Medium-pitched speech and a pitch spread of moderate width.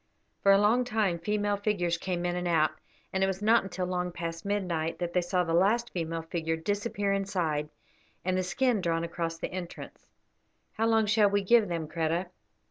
Yes: medium, 180 Hz; average, 3.4 semitones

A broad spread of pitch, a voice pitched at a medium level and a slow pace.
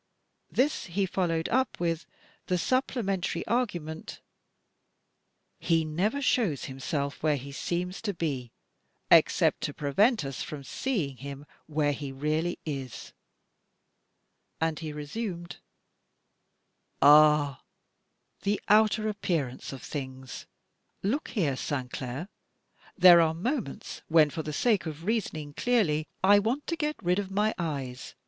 Yes: wide, 5.9 semitones; medium, 165 Hz; slow, 125 wpm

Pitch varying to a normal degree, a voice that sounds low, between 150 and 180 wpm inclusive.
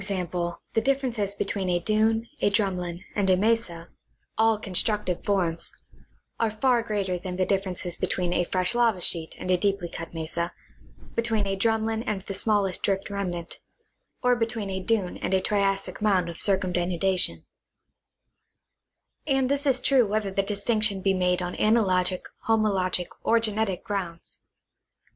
No: average, 3.3 semitones; high, 195 Hz; average, 155 wpm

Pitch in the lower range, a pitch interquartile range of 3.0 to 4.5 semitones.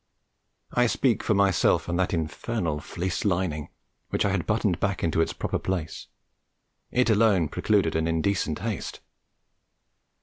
Yes: very low, 95 Hz; average, 4.0 semitones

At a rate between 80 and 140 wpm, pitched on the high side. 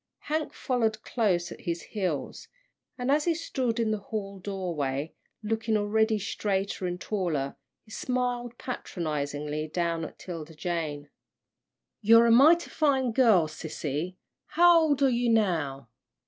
Yes: slow, 135 wpm; high, 205 Hz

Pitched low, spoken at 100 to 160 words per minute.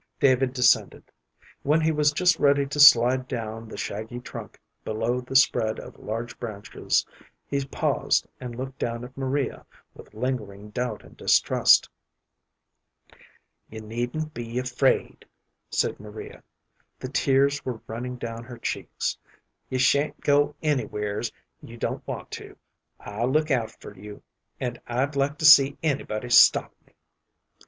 Yes: low, 125 Hz; average, 140 wpm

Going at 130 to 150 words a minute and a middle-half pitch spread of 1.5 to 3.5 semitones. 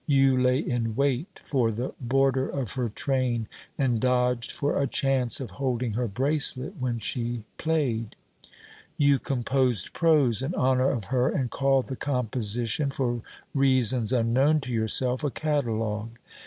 Yes: average, 145 wpm; narrow, 2.4 semitones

